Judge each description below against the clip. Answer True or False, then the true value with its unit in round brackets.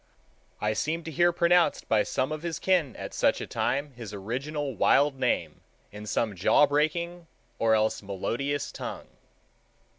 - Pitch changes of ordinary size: False (6.7 semitones)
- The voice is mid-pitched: True (145 Hz)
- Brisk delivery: False (155 wpm)